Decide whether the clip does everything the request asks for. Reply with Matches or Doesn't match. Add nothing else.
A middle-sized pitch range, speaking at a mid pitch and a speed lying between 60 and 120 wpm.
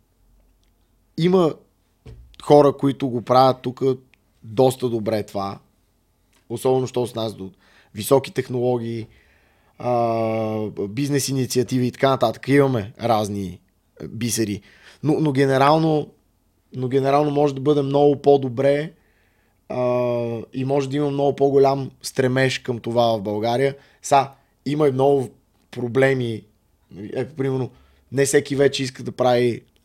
Doesn't match